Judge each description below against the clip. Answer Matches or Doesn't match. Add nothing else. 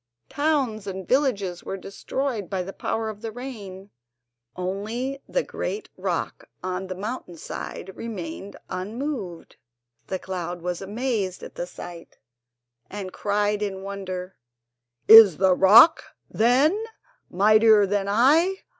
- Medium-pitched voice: Doesn't match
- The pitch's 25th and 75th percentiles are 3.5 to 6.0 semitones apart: Matches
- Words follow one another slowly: Matches